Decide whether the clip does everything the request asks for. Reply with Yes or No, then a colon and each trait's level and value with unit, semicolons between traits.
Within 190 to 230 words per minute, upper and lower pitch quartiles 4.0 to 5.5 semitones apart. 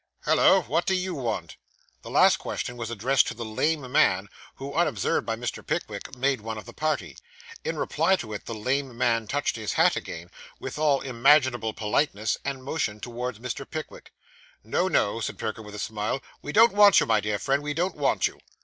Yes: average, 200 wpm; average, 5.1 semitones